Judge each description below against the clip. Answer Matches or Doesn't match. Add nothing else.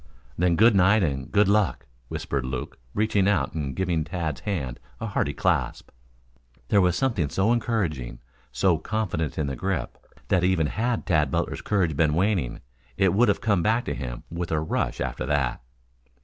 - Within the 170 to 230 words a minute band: Matches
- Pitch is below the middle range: Matches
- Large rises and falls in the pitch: Matches